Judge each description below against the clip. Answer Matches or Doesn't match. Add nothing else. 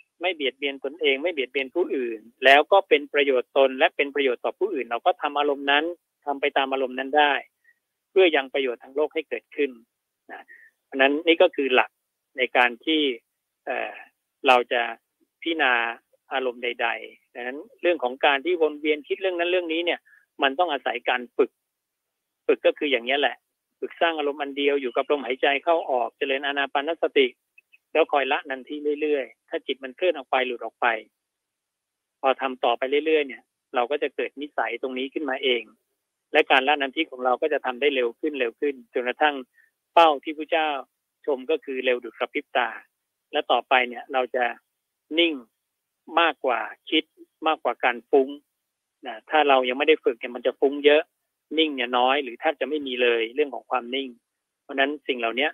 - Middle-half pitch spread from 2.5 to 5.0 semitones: Matches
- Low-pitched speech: Doesn't match